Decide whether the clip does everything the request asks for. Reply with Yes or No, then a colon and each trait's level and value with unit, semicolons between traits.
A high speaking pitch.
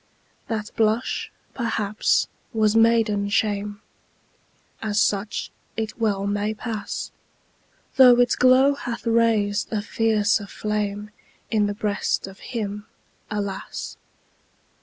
Yes: high, 215 Hz